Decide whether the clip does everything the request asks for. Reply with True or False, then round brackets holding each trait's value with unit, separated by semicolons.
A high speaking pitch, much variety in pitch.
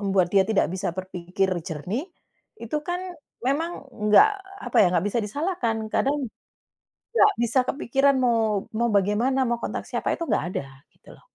True (230 Hz; 6.0 semitones)